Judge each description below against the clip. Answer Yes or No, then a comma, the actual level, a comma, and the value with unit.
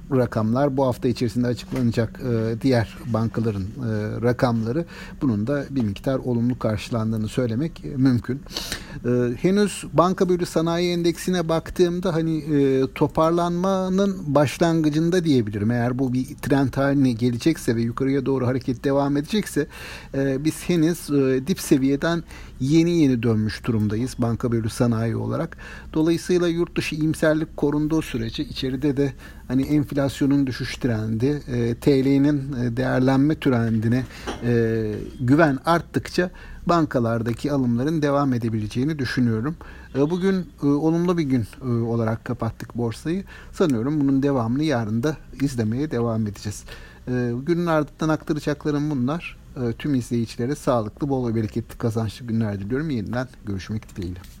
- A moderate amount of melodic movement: Yes, average, 4.7 semitones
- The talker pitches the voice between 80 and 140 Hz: Yes, low, 135 Hz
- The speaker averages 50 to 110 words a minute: No, average, 120 wpm